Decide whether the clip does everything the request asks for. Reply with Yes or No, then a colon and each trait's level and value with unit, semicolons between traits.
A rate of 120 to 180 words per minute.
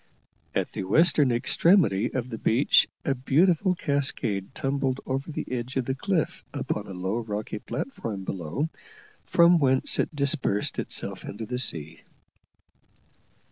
Yes: average, 140 wpm